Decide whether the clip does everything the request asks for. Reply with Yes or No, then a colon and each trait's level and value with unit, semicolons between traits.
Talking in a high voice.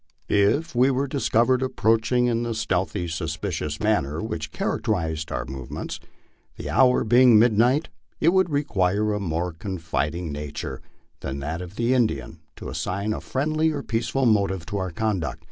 No: low, 105 Hz